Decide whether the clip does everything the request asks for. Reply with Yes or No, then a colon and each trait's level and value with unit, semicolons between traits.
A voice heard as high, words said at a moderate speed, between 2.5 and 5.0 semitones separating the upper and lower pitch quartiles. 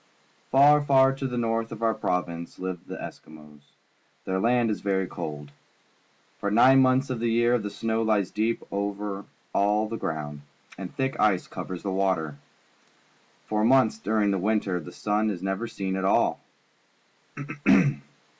No: low, 105 Hz; average, 155 wpm; average, 3.6 semitones